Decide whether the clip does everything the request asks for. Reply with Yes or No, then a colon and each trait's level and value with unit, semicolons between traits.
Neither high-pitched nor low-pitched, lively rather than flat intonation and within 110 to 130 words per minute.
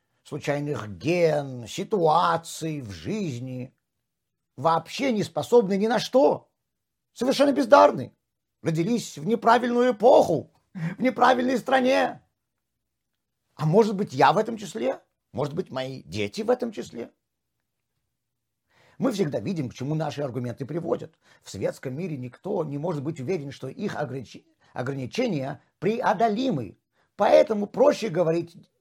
Yes: medium, 165 Hz; wide, 8.3 semitones; average, 120 wpm